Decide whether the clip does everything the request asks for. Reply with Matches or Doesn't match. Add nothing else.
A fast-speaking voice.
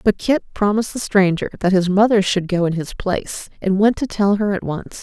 Matches